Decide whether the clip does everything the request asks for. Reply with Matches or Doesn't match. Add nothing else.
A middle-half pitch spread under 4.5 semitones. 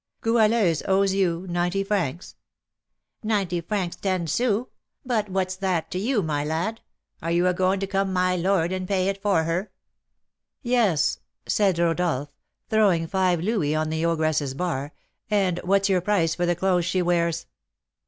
Matches